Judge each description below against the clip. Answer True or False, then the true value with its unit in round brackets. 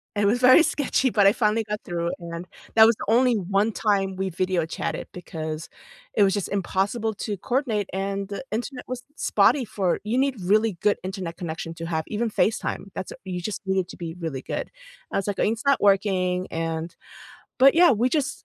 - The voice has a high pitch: True (200 Hz)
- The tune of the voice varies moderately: True (3.9 semitones)